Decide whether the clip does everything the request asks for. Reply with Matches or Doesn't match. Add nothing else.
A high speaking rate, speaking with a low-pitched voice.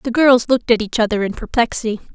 Doesn't match